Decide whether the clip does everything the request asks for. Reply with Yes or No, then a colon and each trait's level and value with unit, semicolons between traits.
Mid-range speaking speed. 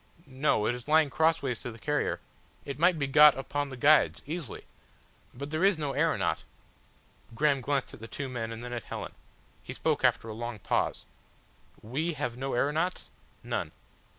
Yes: average, 180 wpm